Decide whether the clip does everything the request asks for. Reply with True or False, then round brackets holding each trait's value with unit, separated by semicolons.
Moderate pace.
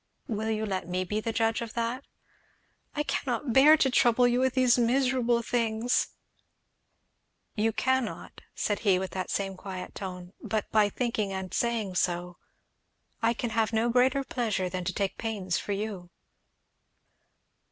True (160 wpm)